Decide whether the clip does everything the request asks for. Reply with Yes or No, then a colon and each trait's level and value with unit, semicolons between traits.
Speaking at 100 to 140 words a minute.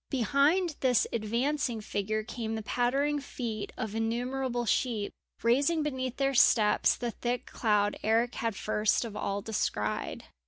Yes: slow, 135 wpm